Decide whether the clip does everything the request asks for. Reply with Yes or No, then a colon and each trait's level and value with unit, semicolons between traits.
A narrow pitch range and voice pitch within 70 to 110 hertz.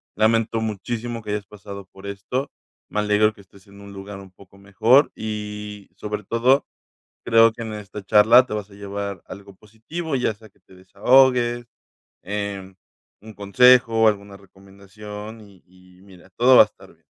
Yes: narrow, 2.3 semitones; low, 105 Hz